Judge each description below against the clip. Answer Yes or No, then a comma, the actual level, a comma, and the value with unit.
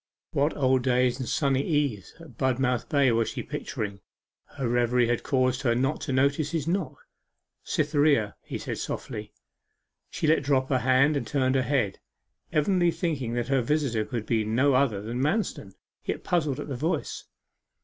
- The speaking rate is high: No, average, 170 wpm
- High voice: No, low, 130 Hz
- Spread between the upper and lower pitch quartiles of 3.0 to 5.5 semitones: Yes, average, 3.3 semitones